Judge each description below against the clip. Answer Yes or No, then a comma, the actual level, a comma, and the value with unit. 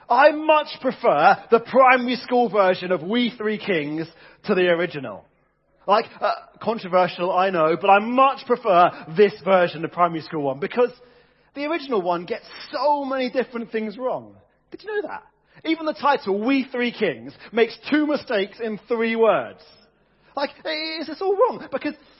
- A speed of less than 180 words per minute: Yes, average, 165 wpm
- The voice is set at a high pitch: Yes, high, 235 Hz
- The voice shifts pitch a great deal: Yes, wide, 6.4 semitones